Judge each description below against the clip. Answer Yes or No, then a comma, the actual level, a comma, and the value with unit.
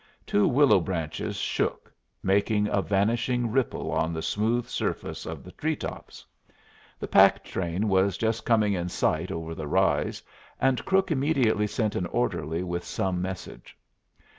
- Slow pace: No, average, 150 wpm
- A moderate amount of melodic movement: Yes, average, 4.8 semitones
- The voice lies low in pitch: Yes, low, 100 Hz